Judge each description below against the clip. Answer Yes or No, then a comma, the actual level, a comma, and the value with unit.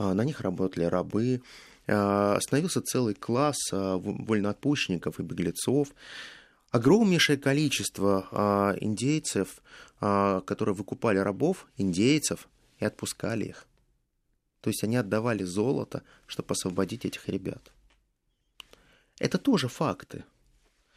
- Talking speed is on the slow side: Yes, slow, 90 wpm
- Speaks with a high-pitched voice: No, low, 105 Hz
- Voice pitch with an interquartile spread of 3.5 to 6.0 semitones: Yes, average, 4.8 semitones